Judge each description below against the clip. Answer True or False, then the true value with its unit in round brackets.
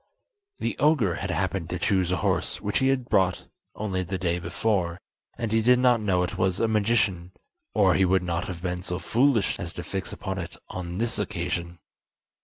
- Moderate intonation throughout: True (3.5 semitones)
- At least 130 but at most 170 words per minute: False (200 wpm)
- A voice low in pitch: True (95 Hz)